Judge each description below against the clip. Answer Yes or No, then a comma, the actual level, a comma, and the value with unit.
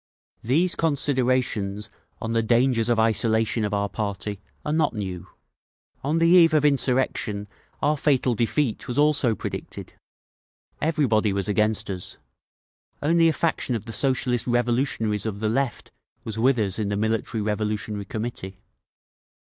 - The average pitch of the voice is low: Yes, low, 115 Hz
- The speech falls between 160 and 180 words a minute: No, average, 140 wpm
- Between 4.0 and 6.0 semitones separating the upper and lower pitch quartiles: Yes, average, 4.5 semitones